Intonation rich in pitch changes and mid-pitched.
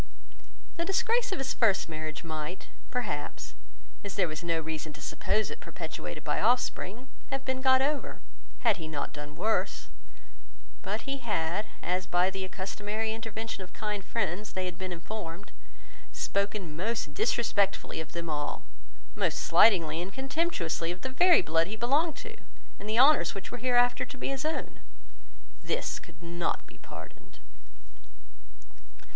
No: wide, 6.6 semitones; high, 200 Hz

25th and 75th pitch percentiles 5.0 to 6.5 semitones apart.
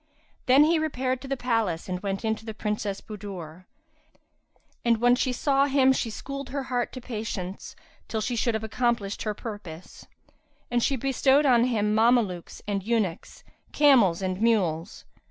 No: average, 4.2 semitones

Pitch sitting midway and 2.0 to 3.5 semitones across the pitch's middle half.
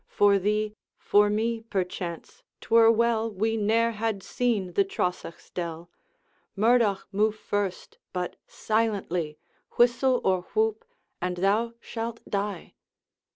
No: high, 210 Hz; average, 3.1 semitones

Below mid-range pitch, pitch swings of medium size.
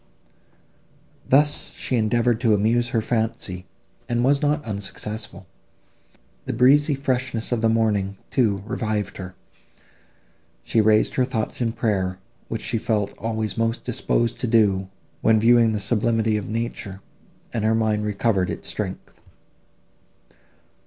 No: low, 110 Hz; narrow, 2.2 semitones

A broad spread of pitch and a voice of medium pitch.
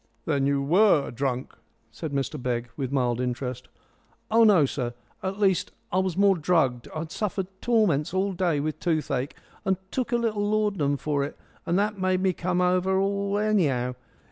Yes: wide, 6.3 semitones; medium, 175 Hz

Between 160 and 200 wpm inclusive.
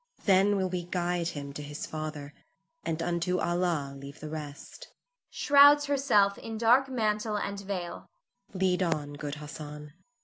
No: average, 145 wpm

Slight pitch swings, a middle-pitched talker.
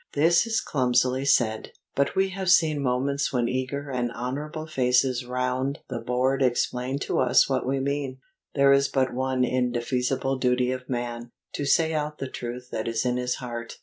No: narrow, 2.0 semitones; low, 130 Hz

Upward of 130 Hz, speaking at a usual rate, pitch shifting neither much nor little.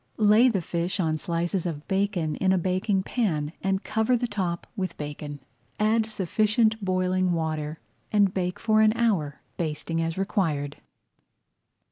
Yes: medium, 185 Hz; average, 145 wpm; average, 4.4 semitones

